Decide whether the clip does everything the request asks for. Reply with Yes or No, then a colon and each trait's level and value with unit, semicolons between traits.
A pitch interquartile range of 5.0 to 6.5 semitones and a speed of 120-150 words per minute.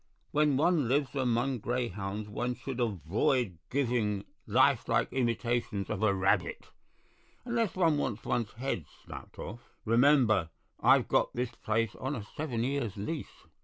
No: average, 4.3 semitones; average, 140 wpm